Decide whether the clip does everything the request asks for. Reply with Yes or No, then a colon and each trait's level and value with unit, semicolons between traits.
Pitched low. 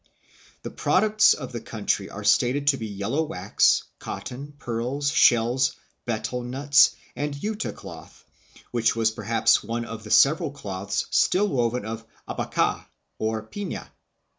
Yes: low, 120 Hz